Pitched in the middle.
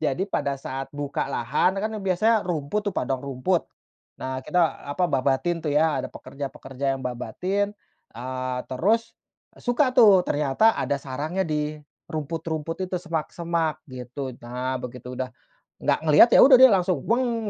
Yes: medium, 155 Hz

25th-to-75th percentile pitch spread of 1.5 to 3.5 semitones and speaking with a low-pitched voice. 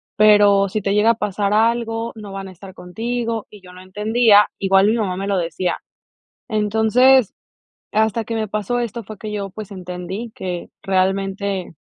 No: narrow, 2.5 semitones; high, 205 Hz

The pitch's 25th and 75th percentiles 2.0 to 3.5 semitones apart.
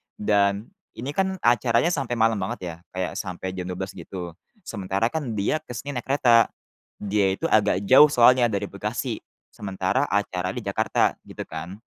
No: average, 4.3 semitones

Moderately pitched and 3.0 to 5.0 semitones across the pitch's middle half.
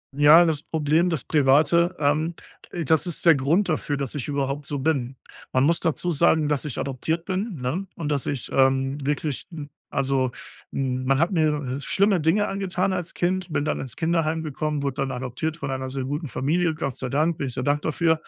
Yes: medium, 150 Hz; average, 3.4 semitones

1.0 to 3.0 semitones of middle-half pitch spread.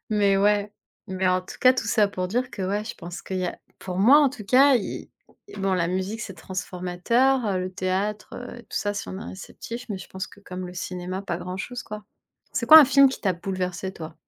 No: average, 3.5 semitones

